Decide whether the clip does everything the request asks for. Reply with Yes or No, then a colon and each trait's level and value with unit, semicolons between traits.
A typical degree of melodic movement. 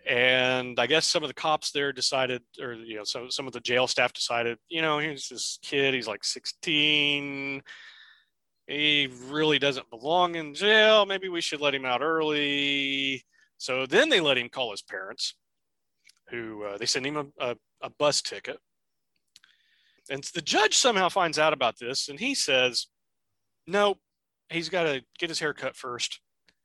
Yes: average, 3.9 semitones